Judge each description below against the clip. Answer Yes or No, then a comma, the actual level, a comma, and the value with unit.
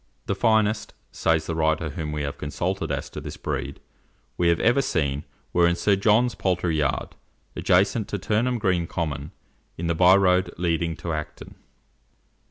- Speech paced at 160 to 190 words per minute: Yes, average, 165 wpm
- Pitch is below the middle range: Yes, very low, 85 Hz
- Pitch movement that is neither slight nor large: Yes, average, 3.9 semitones